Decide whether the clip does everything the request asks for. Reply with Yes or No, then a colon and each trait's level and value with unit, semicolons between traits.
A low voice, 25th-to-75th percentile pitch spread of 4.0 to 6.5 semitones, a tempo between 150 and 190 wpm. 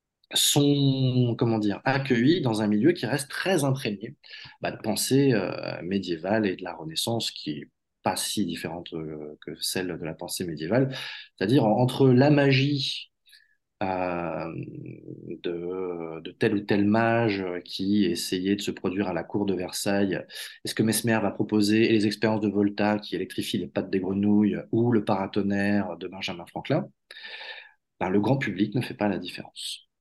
Yes: low, 105 Hz; average, 4.8 semitones; average, 170 wpm